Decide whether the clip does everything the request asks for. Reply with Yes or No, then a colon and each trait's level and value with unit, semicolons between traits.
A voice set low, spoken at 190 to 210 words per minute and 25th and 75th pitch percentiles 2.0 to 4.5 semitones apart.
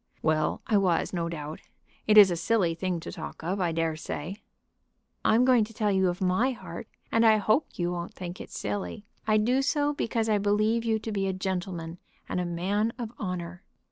No: high, 195 Hz; fast, 205 wpm; average, 4.0 semitones